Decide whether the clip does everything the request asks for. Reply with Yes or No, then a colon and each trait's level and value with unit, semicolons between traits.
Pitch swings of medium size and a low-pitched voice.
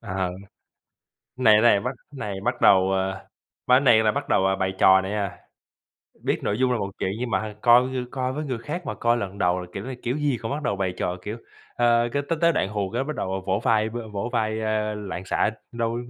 Yes: average, 4.1 semitones; low, 110 Hz